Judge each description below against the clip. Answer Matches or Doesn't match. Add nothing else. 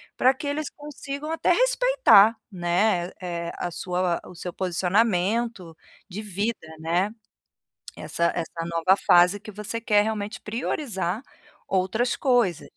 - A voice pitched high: Matches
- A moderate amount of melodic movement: Matches